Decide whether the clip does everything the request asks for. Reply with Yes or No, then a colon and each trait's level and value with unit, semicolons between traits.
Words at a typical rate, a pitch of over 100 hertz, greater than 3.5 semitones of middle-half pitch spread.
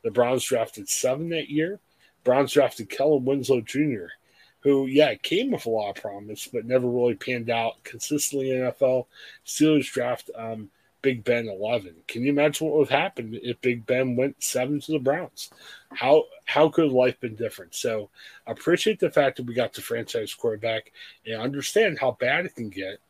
Yes: average, 185 wpm; low, 135 Hz; average, 4.2 semitones